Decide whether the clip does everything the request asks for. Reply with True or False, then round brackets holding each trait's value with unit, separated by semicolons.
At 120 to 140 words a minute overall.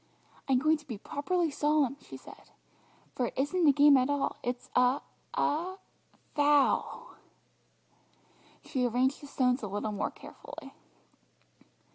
True (135 wpm)